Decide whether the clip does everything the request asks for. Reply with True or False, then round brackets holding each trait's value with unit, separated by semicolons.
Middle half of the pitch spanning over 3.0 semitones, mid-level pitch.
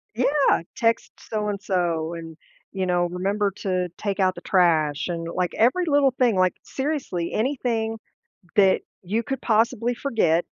False (4.9 semitones; 200 Hz)